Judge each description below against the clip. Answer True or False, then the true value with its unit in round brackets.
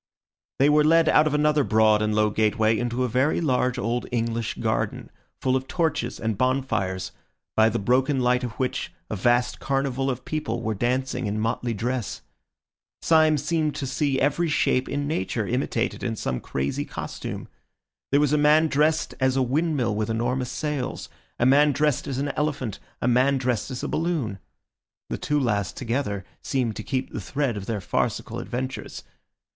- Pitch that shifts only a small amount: False (4.2 semitones)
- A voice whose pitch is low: True (130 Hz)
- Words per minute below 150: False (175 wpm)